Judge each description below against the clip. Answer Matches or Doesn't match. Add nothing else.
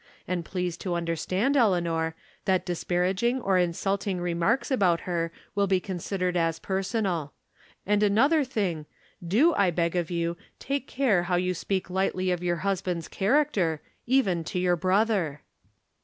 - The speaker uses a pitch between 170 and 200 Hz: Matches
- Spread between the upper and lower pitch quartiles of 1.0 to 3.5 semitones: Matches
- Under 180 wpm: Matches